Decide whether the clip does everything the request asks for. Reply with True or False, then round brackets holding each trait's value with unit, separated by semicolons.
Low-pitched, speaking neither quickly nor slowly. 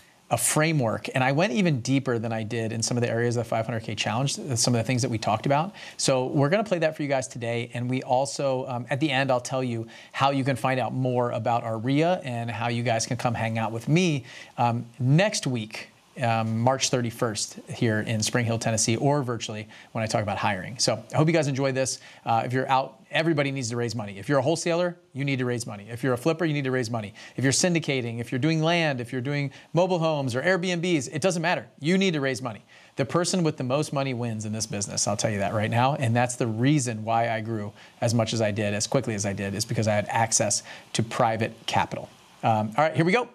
False (125 Hz; 255 wpm)